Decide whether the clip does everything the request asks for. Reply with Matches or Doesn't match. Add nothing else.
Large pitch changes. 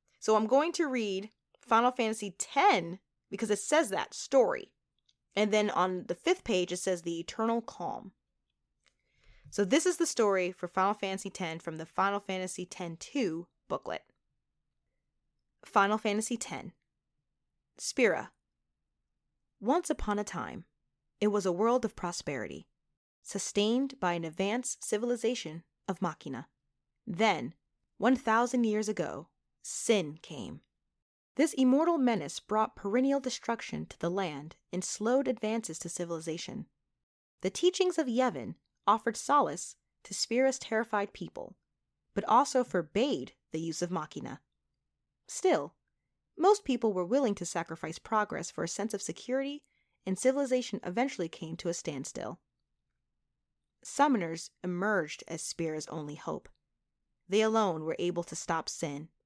Matches